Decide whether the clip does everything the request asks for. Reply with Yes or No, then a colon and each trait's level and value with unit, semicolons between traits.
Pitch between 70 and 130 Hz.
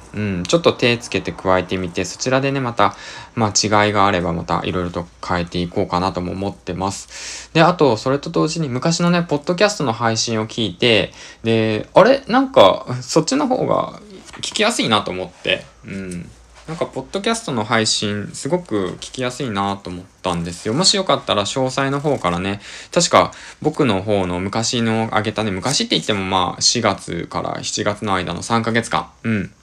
Yes: low, 110 Hz